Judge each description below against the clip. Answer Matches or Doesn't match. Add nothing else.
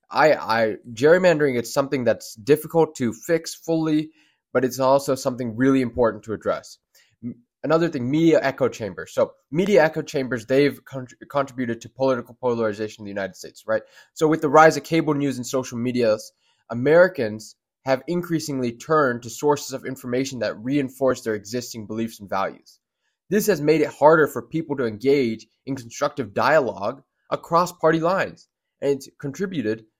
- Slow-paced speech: Doesn't match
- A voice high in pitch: Doesn't match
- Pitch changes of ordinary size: Matches